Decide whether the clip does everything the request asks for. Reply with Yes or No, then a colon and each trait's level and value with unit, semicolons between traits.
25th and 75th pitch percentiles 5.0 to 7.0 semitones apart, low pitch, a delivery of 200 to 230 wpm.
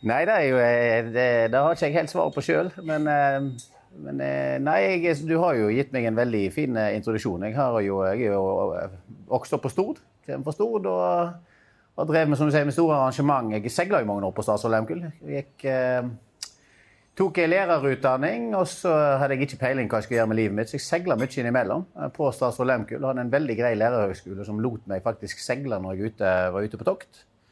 Yes: wide, 5.5 semitones; low, 125 Hz; fast, 205 wpm